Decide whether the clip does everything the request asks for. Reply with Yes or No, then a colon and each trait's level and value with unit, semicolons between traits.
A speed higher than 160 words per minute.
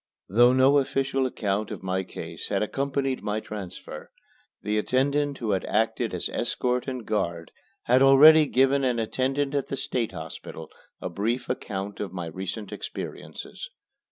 No: average, 155 wpm